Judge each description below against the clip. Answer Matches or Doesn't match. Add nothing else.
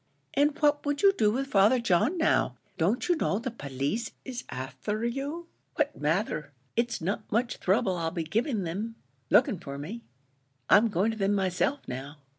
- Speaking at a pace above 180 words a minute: Doesn't match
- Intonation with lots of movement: Matches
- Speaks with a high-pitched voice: Matches